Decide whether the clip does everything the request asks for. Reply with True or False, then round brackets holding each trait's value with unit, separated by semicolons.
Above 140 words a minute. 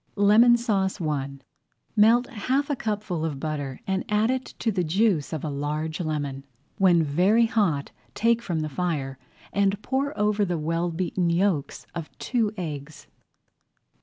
True (155 wpm)